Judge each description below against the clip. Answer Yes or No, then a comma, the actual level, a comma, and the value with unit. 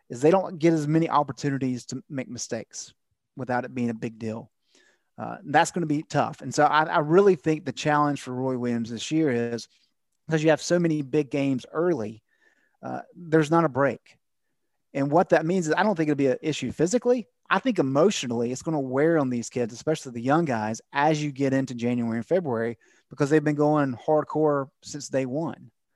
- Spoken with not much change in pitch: No, average, 4.4 semitones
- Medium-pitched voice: Yes, medium, 145 Hz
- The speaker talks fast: Yes, fast, 210 wpm